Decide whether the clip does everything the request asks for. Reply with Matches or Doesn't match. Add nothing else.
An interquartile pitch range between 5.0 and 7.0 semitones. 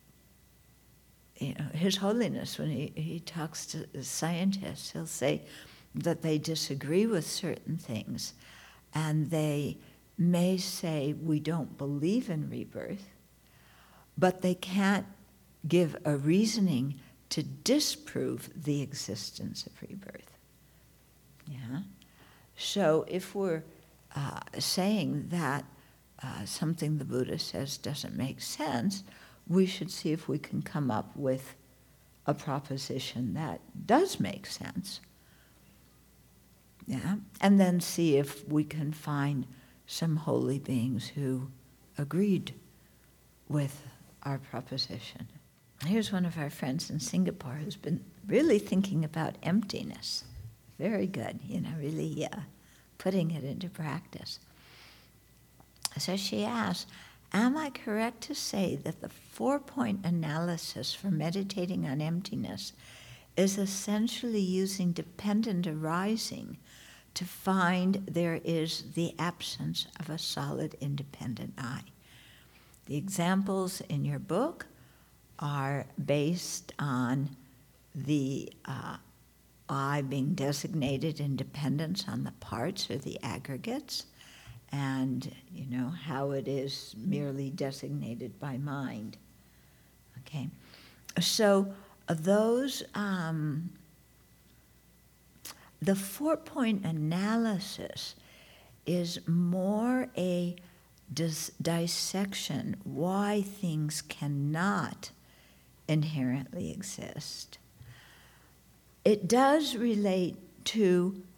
Matches